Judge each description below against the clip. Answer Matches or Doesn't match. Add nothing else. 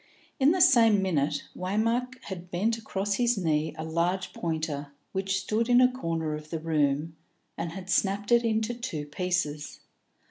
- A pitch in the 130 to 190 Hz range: Matches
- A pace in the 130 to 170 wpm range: Matches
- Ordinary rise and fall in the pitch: Doesn't match